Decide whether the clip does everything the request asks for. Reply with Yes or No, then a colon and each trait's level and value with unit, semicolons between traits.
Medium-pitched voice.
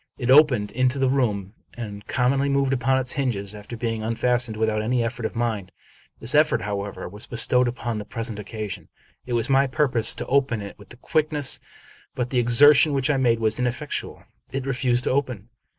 No: low, 120 Hz